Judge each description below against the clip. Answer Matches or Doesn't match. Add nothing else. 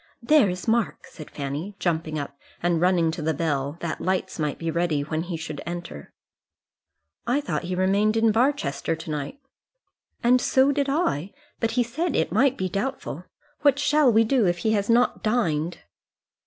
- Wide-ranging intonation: Matches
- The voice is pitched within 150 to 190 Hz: Matches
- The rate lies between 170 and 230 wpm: Matches